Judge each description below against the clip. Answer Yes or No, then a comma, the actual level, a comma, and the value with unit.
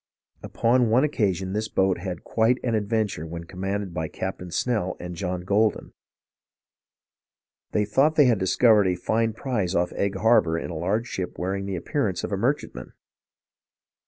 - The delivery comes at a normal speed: Yes, average, 170 wpm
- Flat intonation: No, average, 3.8 semitones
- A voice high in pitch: No, low, 100 Hz